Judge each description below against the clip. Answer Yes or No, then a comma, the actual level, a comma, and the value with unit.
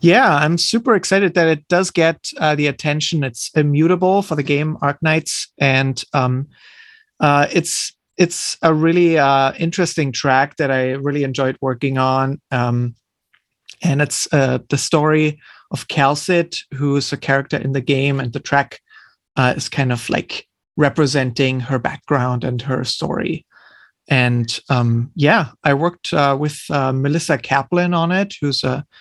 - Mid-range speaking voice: Yes, medium, 145 Hz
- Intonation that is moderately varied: Yes, average, 3.5 semitones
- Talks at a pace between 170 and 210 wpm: No, average, 155 wpm